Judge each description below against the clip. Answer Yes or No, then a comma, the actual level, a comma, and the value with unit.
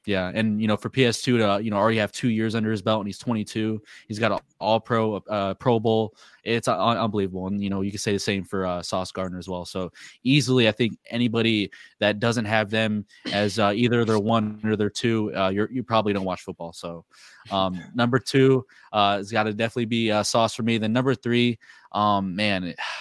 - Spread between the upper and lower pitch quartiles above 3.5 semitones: No, narrow, 2.5 semitones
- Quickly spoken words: Yes, fast, 230 wpm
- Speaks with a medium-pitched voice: No, low, 110 Hz